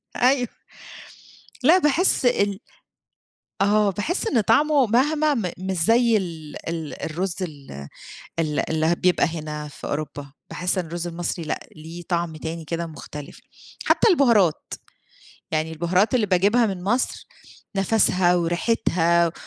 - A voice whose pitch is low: No, medium, 180 Hz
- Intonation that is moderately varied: No, wide, 5.7 semitones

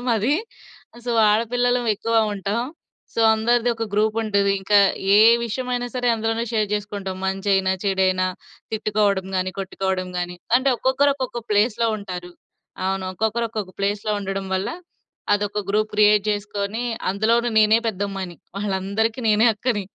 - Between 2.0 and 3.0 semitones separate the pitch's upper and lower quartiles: Yes, average, 2.7 semitones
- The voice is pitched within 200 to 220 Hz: Yes, high, 210 Hz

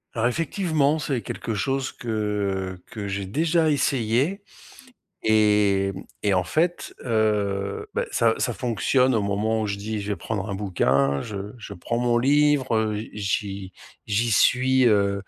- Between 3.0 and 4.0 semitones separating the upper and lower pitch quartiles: No, average, 4.6 semitones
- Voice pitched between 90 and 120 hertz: Yes, low, 110 Hz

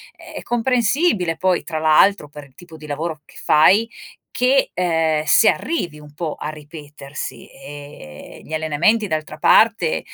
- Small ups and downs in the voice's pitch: No, average, 5.3 semitones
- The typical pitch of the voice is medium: Yes, medium, 160 Hz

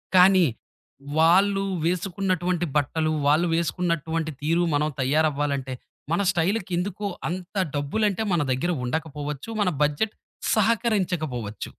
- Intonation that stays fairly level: No, average, 4.1 semitones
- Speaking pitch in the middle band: Yes, medium, 170 Hz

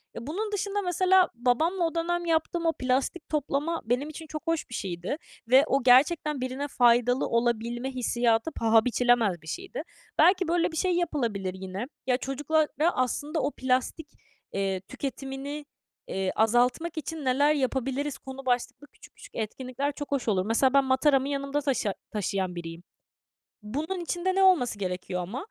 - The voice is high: Yes, very high, 270 Hz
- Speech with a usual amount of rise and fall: Yes, average, 5.0 semitones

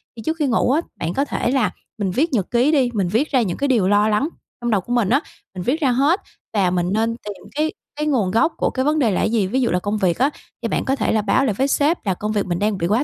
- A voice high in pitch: Yes, high, 230 Hz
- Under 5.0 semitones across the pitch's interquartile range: No, average, 5.3 semitones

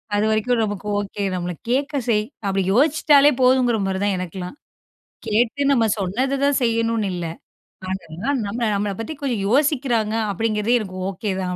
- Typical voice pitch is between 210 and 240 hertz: Yes, high, 220 Hz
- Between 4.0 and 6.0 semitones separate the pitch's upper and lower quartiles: Yes, average, 4.4 semitones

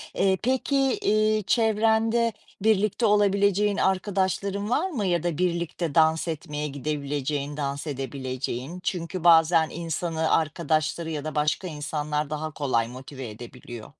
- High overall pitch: No, medium, 165 Hz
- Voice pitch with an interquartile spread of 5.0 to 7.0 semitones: Yes, wide, 5.4 semitones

